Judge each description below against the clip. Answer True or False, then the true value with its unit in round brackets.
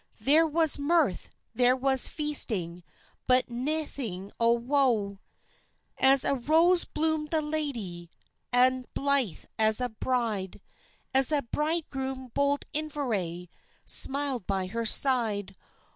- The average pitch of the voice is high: True (260 Hz)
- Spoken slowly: True (115 wpm)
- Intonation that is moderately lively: True (5.0 semitones)